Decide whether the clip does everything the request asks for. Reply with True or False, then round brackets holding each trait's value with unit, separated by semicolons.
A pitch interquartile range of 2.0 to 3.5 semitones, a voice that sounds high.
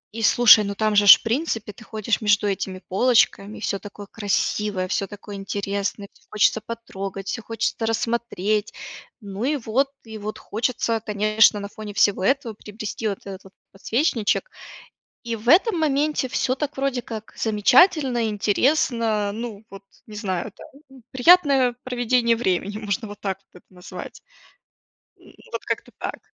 True (3.1 semitones; 220 Hz)